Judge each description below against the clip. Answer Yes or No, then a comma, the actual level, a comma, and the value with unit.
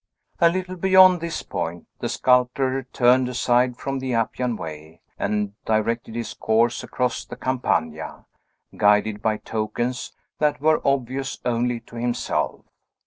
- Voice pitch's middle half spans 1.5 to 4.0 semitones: Yes, average, 3.2 semitones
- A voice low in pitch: Yes, low, 125 Hz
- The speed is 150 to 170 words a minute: No, slow, 135 wpm